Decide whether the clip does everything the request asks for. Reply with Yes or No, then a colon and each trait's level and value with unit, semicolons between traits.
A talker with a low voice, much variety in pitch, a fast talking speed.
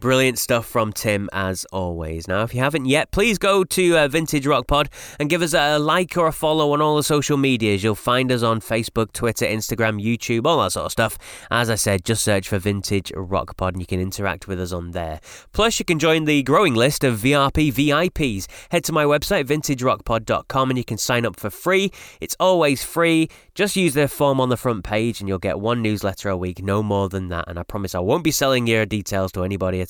Yes: low, 120 Hz; wide, 6.9 semitones; fast, 235 wpm